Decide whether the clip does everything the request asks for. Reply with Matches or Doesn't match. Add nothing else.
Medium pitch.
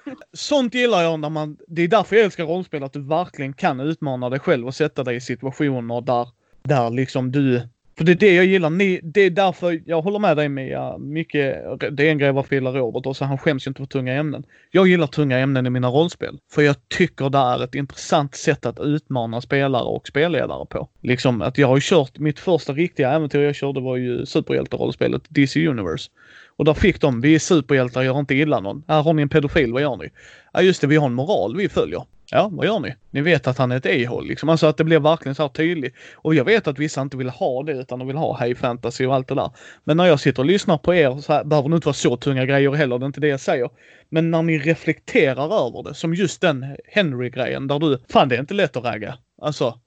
Matches